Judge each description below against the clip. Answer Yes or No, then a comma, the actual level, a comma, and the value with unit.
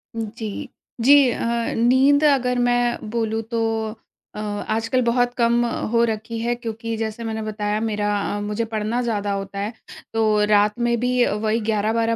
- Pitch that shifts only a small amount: Yes, narrow, 1.9 semitones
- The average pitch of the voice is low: No, high, 225 Hz